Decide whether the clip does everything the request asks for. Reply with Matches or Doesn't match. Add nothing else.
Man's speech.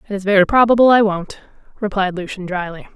Doesn't match